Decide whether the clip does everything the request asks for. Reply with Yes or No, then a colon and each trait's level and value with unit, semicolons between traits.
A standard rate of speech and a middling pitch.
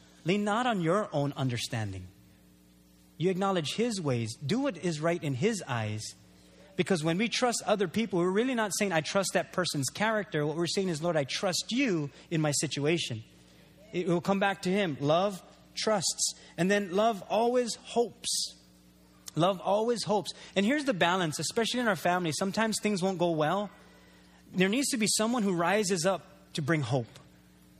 Yes: average, 180 wpm; medium, 180 Hz